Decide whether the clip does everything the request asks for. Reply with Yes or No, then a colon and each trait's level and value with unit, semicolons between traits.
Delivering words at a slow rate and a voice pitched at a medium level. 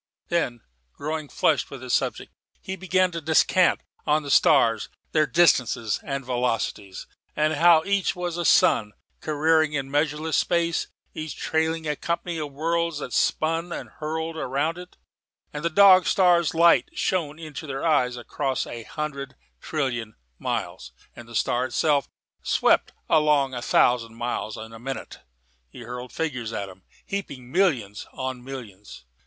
No: average, 150 wpm; medium, 150 Hz